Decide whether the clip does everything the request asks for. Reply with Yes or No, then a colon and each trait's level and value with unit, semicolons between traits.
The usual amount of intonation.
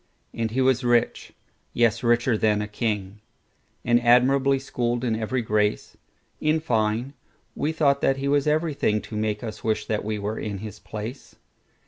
Yes: average, 3.7 semitones